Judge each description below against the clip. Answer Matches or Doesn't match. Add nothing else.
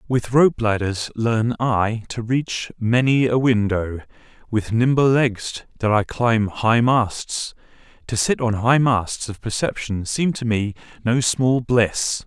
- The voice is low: Matches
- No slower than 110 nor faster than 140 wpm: Doesn't match